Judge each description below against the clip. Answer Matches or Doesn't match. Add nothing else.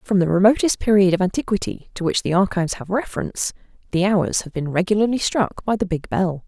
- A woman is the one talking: Matches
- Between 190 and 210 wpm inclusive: Matches